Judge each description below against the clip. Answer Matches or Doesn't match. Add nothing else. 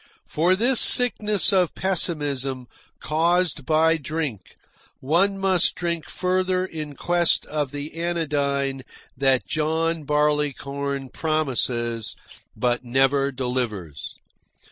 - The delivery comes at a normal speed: Doesn't match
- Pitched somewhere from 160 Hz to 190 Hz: Doesn't match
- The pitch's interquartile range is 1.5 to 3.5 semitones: Doesn't match